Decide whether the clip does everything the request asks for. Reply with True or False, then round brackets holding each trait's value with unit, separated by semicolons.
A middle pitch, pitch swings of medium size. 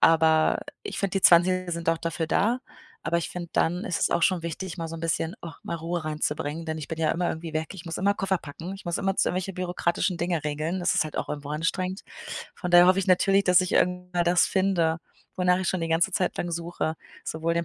False (170 Hz; 2.1 semitones)